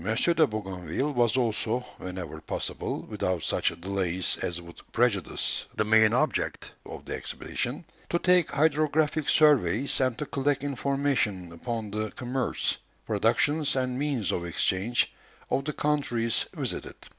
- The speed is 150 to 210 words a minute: No, slow, 135 wpm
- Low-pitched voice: Yes, low, 120 Hz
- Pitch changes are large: Yes, wide, 6.6 semitones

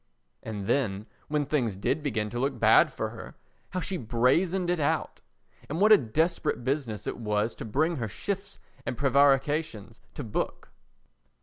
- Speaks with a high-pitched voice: No, low, 135 Hz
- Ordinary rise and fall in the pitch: No, wide, 6.0 semitones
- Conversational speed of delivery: Yes, average, 165 wpm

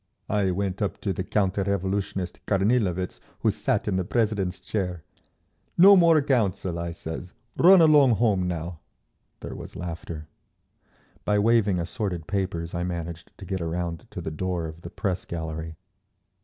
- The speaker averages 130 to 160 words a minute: Yes, average, 155 wpm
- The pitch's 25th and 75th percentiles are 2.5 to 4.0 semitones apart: Yes, average, 3.4 semitones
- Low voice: Yes, very low, 95 Hz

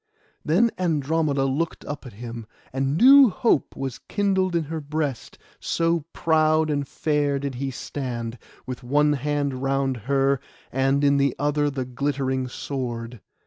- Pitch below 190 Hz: Yes, medium, 140 Hz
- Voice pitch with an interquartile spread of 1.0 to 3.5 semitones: Yes, average, 2.8 semitones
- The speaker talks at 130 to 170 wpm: Yes, average, 145 wpm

